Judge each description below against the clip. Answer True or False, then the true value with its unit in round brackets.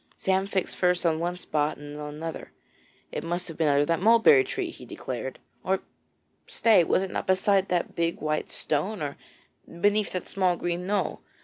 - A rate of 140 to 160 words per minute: False (190 wpm)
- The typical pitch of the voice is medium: True (180 Hz)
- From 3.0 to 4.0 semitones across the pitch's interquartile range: True (3.6 semitones)